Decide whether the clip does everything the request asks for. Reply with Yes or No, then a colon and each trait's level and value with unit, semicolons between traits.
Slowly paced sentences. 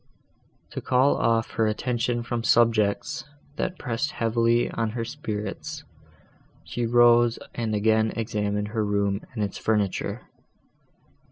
Yes: slow, 120 wpm